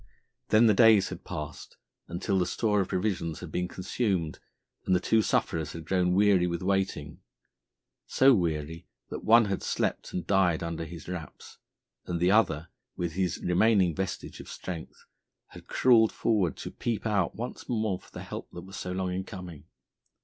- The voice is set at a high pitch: No, very low, 90 Hz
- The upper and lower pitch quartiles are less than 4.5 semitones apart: Yes, average, 3.4 semitones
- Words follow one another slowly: No, average, 175 wpm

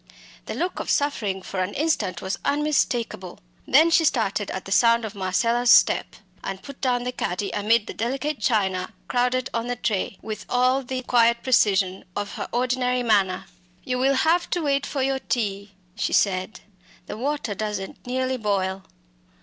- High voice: Yes, high, 235 Hz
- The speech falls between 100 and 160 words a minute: No, average, 170 wpm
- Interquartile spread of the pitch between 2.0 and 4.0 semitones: No, average, 4.5 semitones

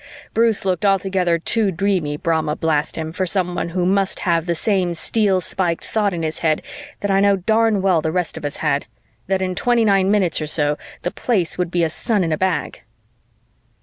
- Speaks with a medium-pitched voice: Yes, medium, 180 Hz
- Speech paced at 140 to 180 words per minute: No, fast, 205 wpm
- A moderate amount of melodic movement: Yes, average, 3.2 semitones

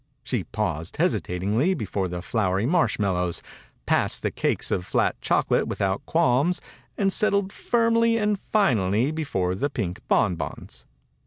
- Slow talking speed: Yes, slow, 130 wpm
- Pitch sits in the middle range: No, low, 115 Hz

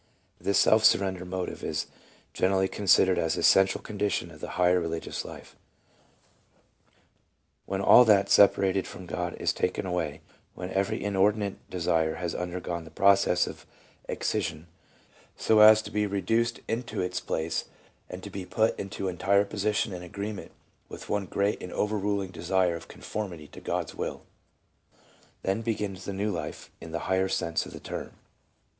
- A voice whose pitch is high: No, very low, 95 Hz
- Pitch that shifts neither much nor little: No, narrow, 2.3 semitones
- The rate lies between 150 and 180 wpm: Yes, average, 160 wpm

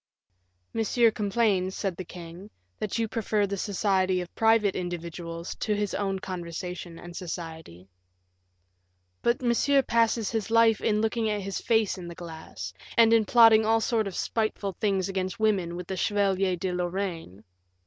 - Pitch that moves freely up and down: No, average, 3.8 semitones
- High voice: Yes, high, 195 Hz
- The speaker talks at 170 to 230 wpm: No, average, 160 wpm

